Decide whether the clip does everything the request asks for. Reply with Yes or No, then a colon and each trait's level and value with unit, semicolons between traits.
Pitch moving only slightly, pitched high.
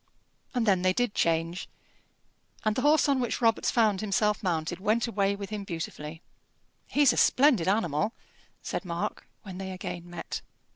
No: average, 4.3 semitones; high, 200 Hz